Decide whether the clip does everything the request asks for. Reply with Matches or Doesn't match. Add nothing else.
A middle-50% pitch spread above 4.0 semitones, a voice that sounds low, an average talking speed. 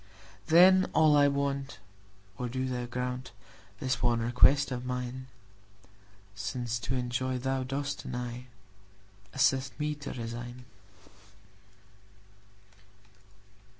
Doesn't match